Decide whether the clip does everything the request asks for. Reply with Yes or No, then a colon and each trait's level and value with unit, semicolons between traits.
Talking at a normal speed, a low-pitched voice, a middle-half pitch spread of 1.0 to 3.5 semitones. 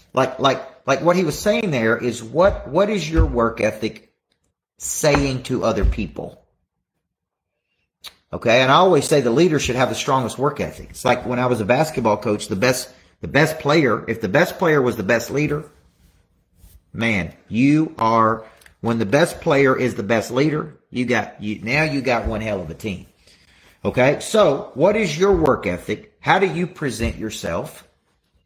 No: average, 185 wpm; low, 120 Hz; average, 5.2 semitones